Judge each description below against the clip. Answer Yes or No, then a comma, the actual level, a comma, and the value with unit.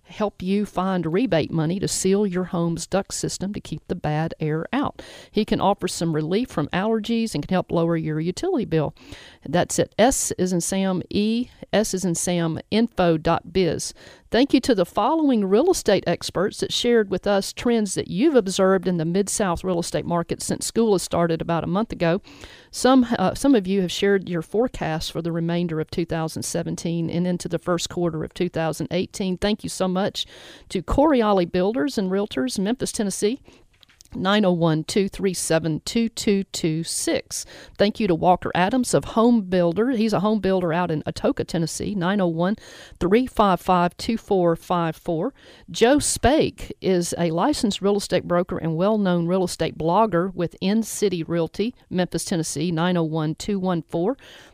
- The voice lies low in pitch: No, medium, 185 Hz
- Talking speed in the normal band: Yes, average, 155 wpm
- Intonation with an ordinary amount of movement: Yes, average, 3.6 semitones